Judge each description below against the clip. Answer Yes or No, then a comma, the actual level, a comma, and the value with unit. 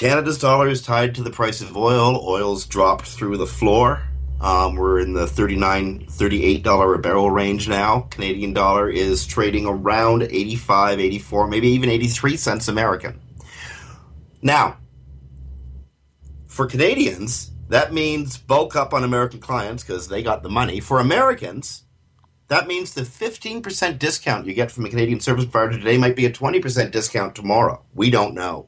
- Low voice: Yes, low, 110 Hz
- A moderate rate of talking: Yes, average, 160 wpm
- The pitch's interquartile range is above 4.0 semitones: Yes, average, 4.4 semitones